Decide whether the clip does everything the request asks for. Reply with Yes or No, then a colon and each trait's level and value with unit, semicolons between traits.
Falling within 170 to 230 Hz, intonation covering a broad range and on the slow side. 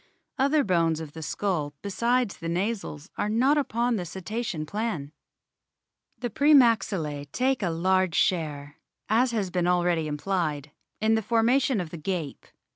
No: high, 190 Hz; wide, 6.2 semitones; average, 150 wpm